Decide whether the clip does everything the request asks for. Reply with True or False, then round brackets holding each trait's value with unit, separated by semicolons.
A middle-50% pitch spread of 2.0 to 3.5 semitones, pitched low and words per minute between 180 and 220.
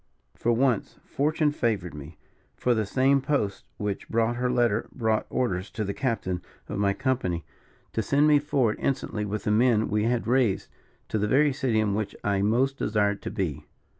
False (4.1 semitones; 110 Hz; 185 wpm)